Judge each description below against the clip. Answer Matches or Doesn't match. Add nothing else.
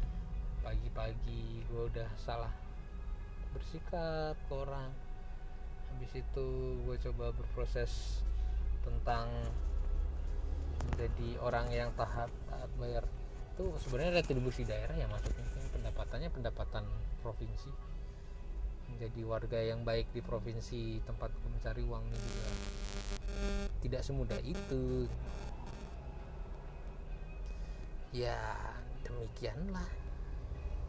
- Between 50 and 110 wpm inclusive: Matches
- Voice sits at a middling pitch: Doesn't match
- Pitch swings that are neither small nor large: Doesn't match